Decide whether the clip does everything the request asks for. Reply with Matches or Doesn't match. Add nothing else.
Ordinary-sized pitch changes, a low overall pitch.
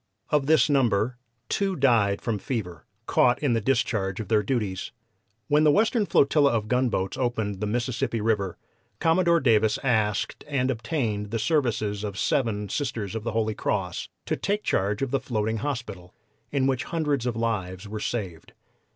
Matches